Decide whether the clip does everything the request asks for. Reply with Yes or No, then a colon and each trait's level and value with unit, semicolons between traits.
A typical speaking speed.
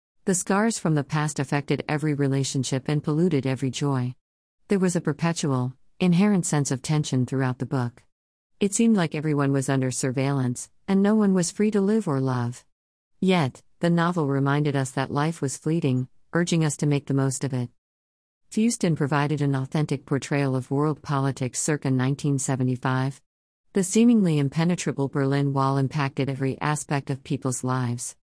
Yes: average, 165 wpm